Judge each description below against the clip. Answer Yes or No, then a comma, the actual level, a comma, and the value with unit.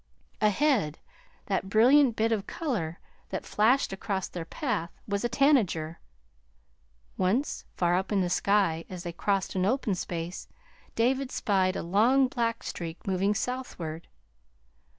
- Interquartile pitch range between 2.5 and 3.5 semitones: No, average, 5.1 semitones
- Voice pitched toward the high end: Yes, high, 200 Hz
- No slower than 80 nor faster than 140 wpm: Yes, slow, 135 wpm